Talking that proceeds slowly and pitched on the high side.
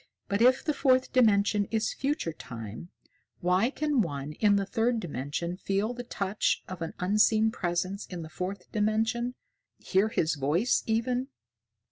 No: average, 150 wpm; high, 205 Hz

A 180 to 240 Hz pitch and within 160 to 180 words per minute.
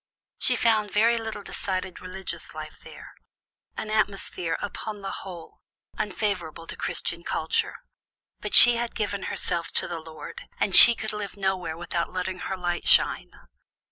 No: high, 190 Hz; average, 150 wpm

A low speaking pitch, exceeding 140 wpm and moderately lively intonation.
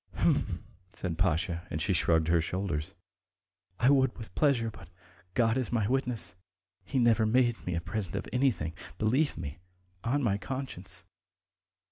No: low, 110 Hz; average, 150 wpm; wide, 6.3 semitones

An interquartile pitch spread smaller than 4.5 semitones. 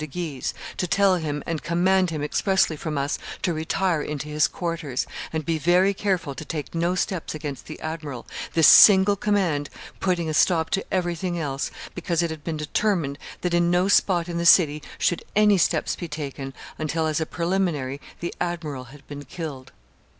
Yes: average, 3.1 semitones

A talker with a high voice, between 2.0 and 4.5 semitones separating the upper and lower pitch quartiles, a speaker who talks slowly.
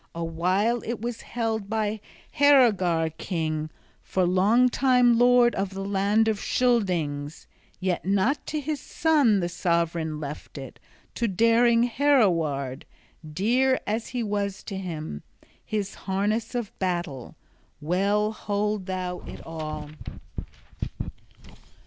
No: high, 200 Hz; wide, 5.4 semitones; slow, 120 wpm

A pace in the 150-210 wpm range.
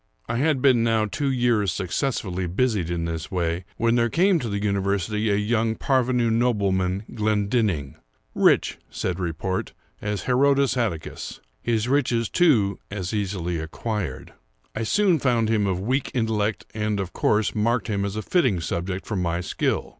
Yes: average, 155 wpm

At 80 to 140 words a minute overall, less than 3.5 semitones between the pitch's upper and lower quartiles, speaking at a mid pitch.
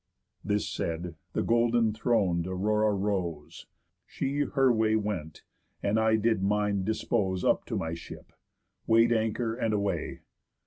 No: slow, 135 wpm; average, 3.0 semitones; low, 105 Hz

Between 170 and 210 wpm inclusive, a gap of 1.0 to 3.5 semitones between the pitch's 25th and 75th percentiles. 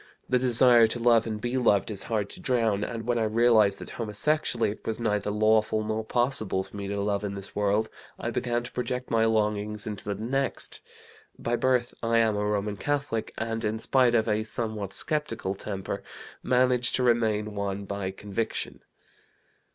Yes: average, 180 wpm; narrow, 2.5 semitones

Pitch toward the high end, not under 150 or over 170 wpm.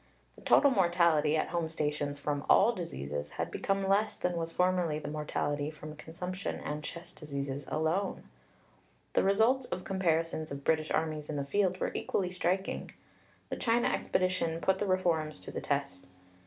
No: medium, 165 Hz; average, 165 wpm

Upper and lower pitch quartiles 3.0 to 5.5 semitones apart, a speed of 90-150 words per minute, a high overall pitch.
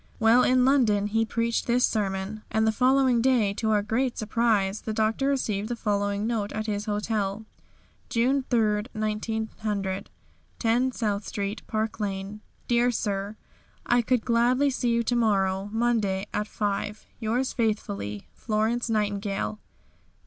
No: narrow, 2.5 semitones; average, 140 wpm; high, 220 Hz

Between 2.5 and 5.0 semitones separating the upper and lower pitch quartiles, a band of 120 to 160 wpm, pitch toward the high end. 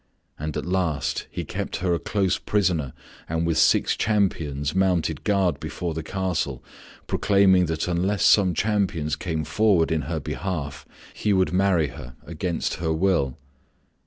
No: average, 3.2 semitones; average, 150 wpm; very low, 85 Hz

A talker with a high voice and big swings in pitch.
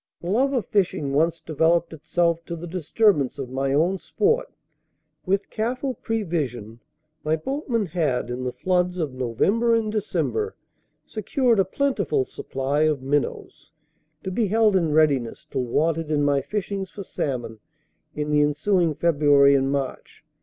No: medium, 165 Hz; wide, 6.3 semitones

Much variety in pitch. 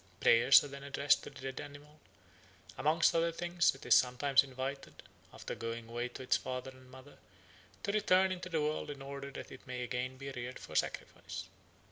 No: average, 2.7 semitones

